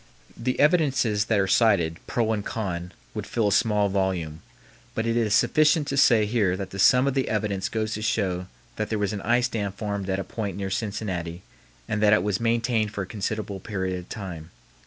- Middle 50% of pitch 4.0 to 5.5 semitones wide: No, average, 3.1 semitones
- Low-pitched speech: Yes, low, 105 Hz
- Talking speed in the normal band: No, fast, 210 wpm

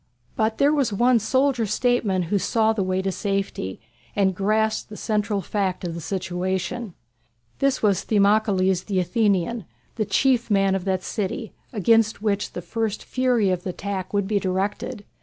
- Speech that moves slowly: No, average, 165 wpm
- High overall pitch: Yes, high, 205 Hz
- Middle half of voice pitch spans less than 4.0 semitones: Yes, average, 2.9 semitones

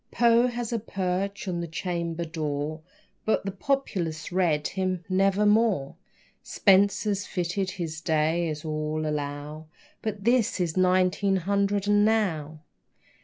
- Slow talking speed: Yes, slow, 125 wpm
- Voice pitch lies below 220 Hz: Yes, medium, 185 Hz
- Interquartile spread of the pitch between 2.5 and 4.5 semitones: Yes, average, 4.2 semitones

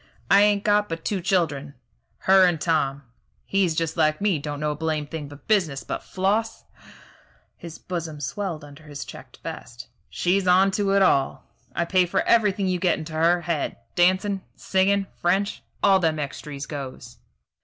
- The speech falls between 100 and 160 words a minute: No, average, 175 wpm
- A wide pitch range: No, average, 4.3 semitones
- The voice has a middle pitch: Yes, medium, 170 Hz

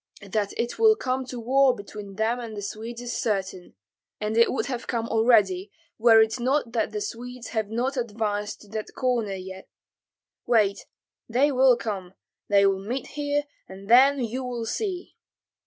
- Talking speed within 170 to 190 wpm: Yes, average, 175 wpm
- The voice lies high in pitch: Yes, high, 230 Hz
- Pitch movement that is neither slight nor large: Yes, average, 3.5 semitones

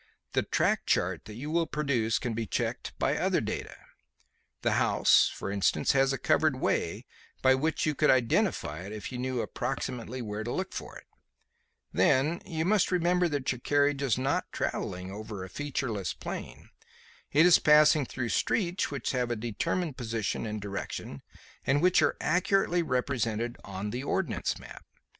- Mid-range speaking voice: No, low, 130 Hz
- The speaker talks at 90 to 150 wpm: No, average, 170 wpm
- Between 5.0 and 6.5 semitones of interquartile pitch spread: Yes, wide, 5.5 semitones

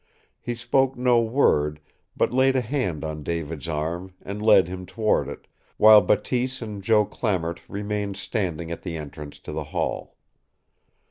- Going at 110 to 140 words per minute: No, average, 155 wpm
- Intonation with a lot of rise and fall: Yes, wide, 6.0 semitones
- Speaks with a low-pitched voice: Yes, low, 100 Hz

